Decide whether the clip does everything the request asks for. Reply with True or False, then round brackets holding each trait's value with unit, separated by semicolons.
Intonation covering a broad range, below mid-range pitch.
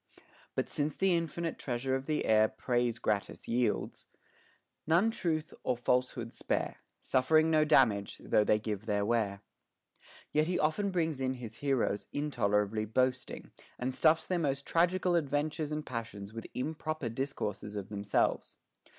True (6.2 semitones; 130 Hz)